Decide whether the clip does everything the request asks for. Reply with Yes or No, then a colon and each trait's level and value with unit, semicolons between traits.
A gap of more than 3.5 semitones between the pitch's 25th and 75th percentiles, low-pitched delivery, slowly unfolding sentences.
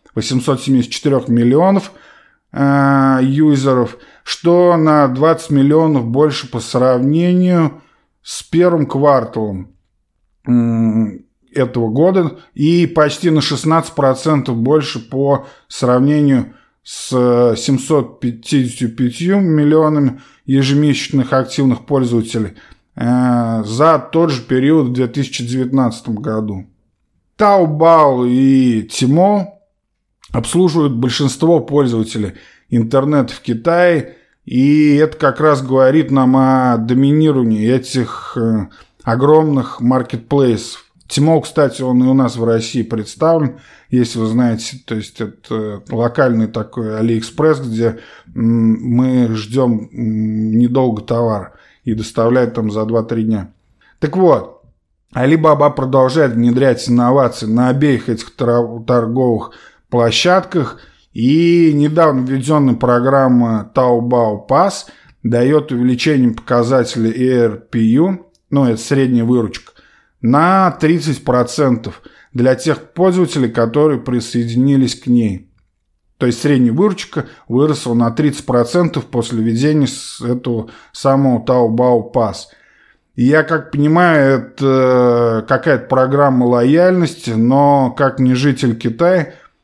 Yes: average, 4.0 semitones; low, 130 Hz; slow, 100 wpm